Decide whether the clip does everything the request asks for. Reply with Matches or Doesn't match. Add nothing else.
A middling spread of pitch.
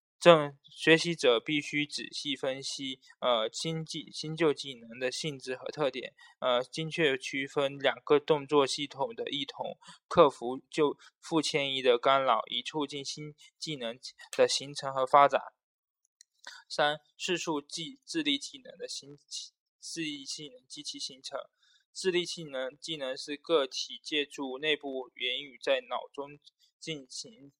Matches